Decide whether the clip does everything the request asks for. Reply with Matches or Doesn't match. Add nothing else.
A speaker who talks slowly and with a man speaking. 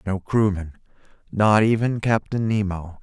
Matches